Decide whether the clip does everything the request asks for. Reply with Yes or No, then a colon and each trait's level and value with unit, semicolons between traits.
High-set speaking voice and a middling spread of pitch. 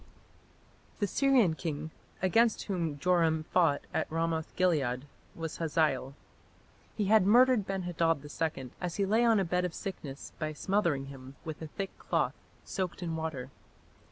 No: medium, 165 Hz; average, 4.0 semitones